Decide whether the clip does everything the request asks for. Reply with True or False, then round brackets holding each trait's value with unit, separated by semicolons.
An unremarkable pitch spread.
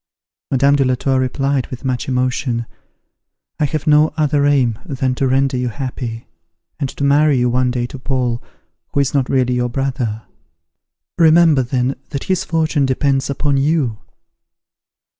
False (2.2 semitones)